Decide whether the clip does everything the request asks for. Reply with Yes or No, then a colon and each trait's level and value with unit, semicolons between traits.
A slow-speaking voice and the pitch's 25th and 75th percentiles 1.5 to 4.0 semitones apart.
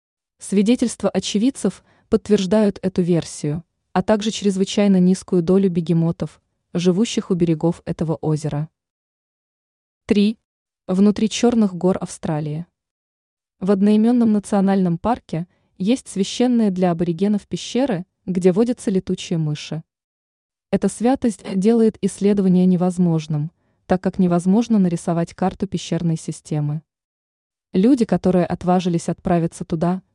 Yes: slow, 100 wpm; average, 3.4 semitones